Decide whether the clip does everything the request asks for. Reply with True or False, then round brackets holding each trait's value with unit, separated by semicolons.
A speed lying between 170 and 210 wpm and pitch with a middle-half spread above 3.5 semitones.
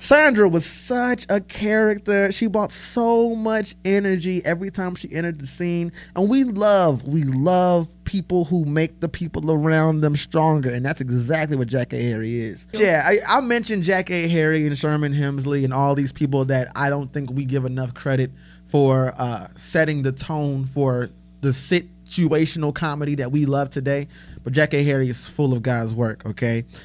True (185 wpm; 5.1 semitones)